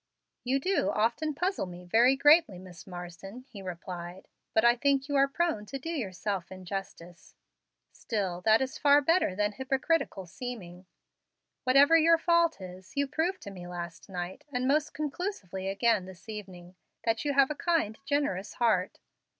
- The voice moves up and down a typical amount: No, wide, 7.4 semitones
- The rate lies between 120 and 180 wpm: Yes, average, 160 wpm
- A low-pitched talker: No, high, 225 Hz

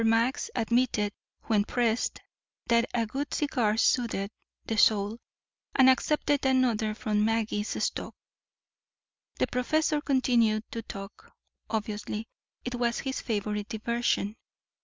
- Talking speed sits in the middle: No, slow, 115 wpm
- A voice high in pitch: Yes, high, 230 Hz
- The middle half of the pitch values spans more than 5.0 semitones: No, average, 2.9 semitones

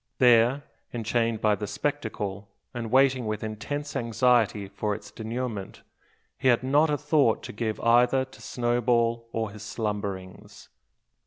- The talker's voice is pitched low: Yes, low, 115 Hz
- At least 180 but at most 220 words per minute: No, average, 140 wpm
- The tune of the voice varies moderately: Yes, average, 3.0 semitones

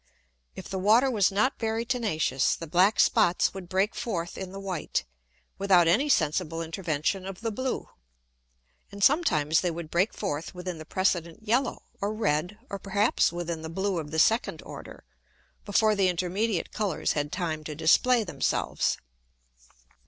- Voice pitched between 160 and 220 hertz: Yes, high, 190 Hz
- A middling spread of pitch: Yes, average, 4.3 semitones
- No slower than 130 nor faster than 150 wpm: No, average, 160 wpm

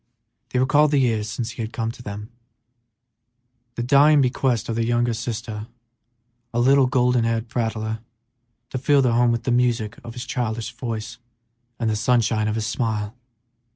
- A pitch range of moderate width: No, narrow, 2.1 semitones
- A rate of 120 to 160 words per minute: No, average, 170 wpm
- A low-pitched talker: Yes, low, 120 Hz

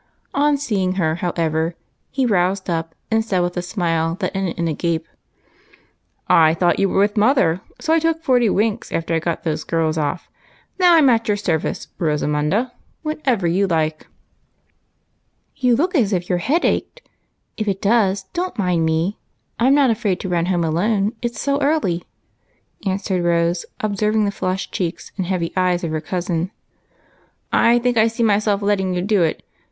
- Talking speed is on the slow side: No, average, 190 wpm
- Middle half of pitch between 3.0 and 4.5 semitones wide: No, average, 5.0 semitones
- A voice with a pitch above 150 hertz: Yes, high, 190 Hz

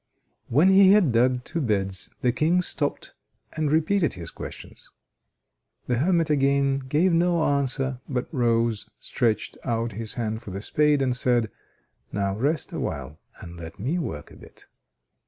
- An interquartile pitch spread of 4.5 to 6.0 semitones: Yes, wide, 5.4 semitones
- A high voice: No, low, 130 Hz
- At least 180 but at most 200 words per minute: No, average, 155 wpm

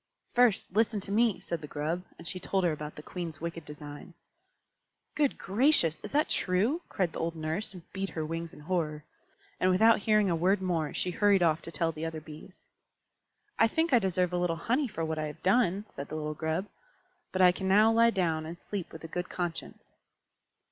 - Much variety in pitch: No, average, 3.9 semitones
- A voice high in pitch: No, medium, 180 Hz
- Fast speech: Yes, fast, 210 wpm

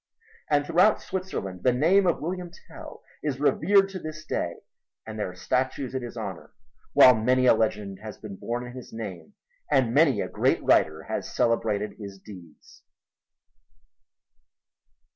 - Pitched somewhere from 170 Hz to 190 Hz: No, low, 125 Hz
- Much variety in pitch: Yes, wide, 6.7 semitones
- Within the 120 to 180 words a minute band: Yes, average, 155 wpm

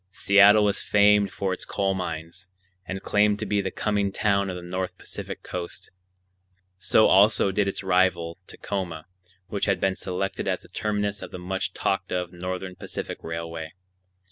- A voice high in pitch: No, very low, 95 Hz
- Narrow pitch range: Yes, narrow, 2.0 semitones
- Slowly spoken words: No, average, 170 wpm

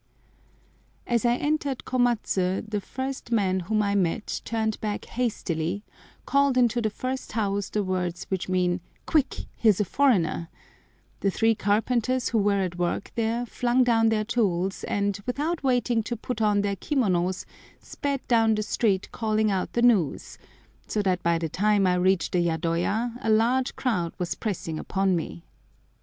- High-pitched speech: Yes, high, 210 Hz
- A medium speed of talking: Yes, average, 160 wpm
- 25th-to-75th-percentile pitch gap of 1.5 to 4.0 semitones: No, average, 4.4 semitones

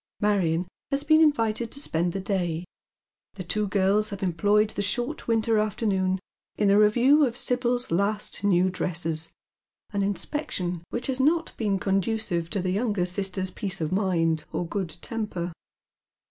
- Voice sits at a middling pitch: No, high, 200 Hz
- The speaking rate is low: No, average, 155 wpm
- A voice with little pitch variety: No, average, 3.8 semitones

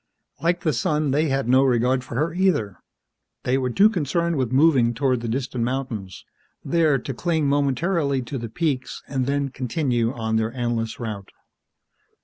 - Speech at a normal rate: Yes, average, 165 wpm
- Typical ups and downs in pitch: Yes, average, 4.1 semitones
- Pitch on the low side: Yes, low, 130 Hz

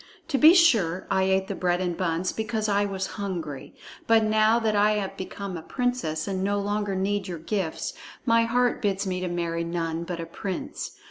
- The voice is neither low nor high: No, high, 195 Hz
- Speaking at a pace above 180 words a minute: Yes, average, 200 wpm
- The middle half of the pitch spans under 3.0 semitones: No, average, 3.5 semitones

